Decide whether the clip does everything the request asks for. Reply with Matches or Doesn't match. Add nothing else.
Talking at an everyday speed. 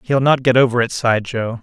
Doesn't match